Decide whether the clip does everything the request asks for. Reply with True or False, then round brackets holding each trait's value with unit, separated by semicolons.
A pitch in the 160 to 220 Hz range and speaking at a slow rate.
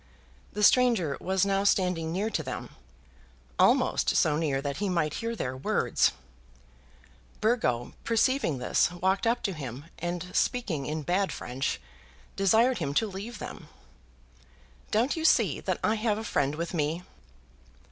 False (185 Hz; 145 wpm)